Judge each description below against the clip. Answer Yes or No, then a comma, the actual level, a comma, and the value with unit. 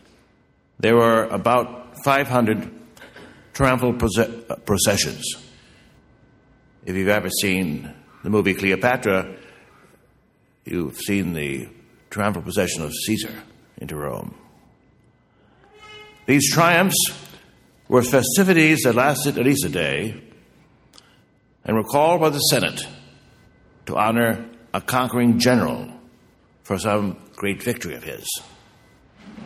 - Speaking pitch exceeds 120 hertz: No, low, 115 Hz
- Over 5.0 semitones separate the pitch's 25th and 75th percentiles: Yes, wide, 5.4 semitones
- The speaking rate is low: Yes, slow, 105 wpm